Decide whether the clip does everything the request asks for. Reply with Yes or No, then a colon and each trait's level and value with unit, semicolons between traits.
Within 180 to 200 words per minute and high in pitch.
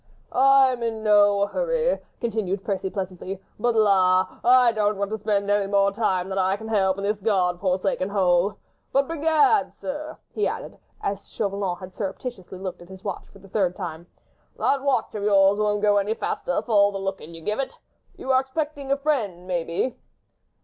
Yes: average, 190 wpm; high, 205 Hz